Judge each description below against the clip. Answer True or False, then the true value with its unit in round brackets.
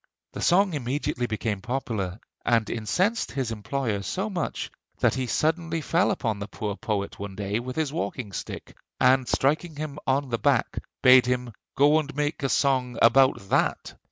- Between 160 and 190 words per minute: True (170 wpm)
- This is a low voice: True (130 Hz)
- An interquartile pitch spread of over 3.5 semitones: True (5.1 semitones)